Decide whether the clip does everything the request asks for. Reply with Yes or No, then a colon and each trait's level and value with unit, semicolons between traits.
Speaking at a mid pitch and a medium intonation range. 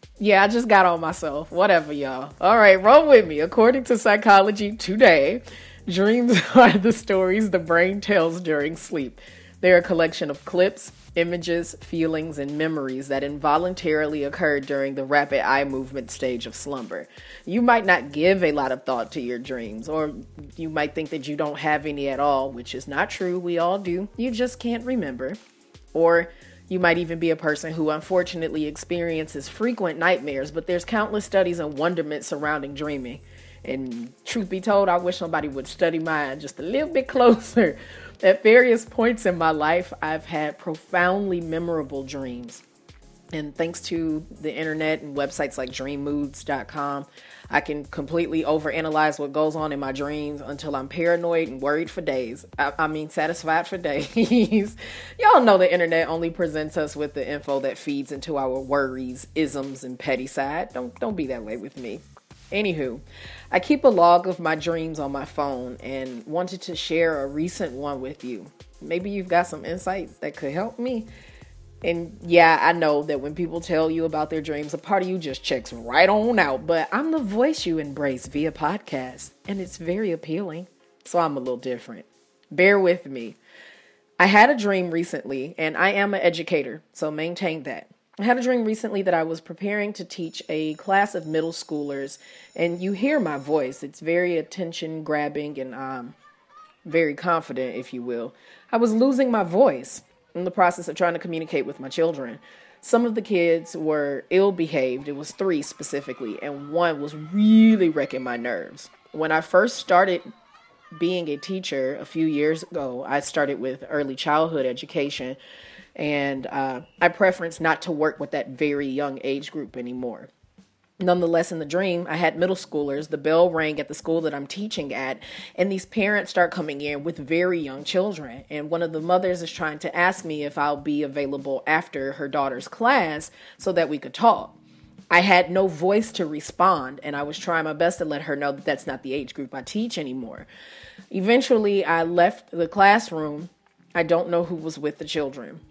Yes: medium, 160 Hz; average, 4.0 semitones